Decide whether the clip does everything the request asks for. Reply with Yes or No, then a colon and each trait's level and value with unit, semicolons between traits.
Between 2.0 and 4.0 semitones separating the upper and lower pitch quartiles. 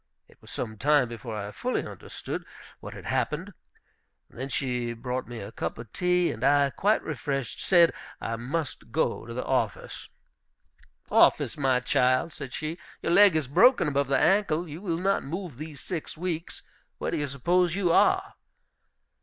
No: wide, 5.4 semitones